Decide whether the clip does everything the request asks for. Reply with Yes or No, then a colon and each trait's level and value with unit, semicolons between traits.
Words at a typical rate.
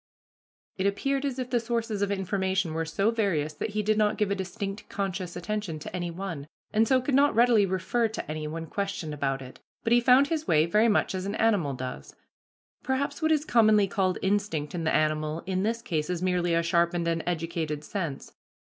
No: fast, 210 wpm